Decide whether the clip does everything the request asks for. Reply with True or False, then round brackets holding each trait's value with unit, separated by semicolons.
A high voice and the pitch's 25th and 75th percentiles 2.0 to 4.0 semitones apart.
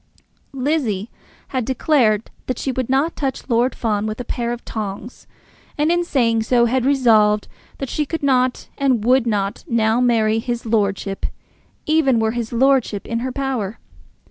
True (240 Hz; 3.3 semitones)